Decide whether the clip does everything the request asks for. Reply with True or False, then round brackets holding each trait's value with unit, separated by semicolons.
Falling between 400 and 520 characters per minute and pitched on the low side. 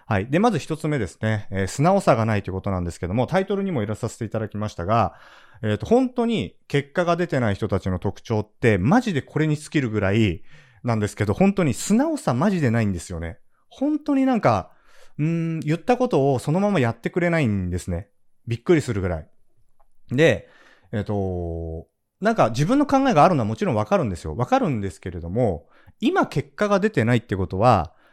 True (420 characters per minute; 120 Hz)